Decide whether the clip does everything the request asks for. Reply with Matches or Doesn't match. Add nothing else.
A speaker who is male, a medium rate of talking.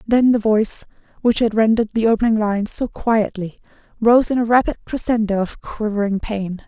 Doesn't match